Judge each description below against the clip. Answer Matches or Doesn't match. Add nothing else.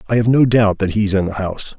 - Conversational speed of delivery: Doesn't match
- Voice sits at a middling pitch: Doesn't match